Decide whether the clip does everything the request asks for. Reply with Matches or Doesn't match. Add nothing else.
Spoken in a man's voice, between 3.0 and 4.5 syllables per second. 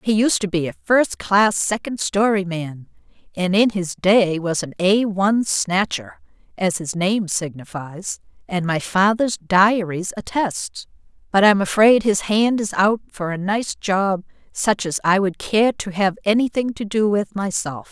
Doesn't match